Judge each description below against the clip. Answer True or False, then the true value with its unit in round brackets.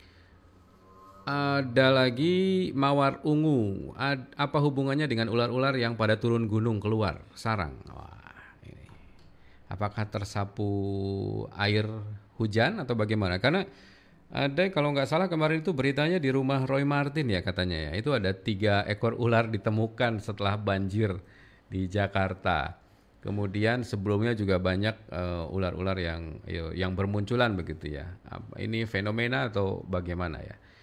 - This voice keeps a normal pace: True (125 wpm)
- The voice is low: True (110 Hz)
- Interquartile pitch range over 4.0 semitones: True (5.2 semitones)